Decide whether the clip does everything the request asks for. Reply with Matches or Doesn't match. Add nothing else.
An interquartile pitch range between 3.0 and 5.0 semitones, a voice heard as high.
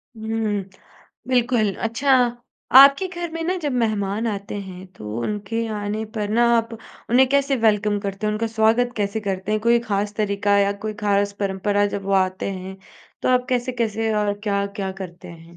Doesn't match